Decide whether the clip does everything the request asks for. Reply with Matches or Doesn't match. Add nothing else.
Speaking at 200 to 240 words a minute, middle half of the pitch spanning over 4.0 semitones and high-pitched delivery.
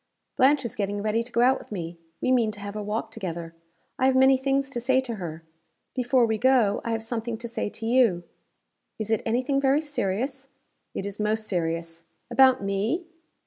Matches